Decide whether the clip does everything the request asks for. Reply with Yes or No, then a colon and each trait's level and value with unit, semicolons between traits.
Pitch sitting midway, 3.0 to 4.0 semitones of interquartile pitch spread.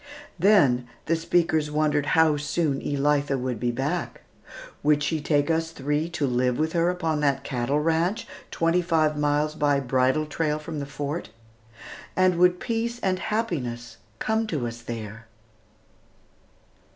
Yes: medium, 150 Hz; average, 3.3 semitones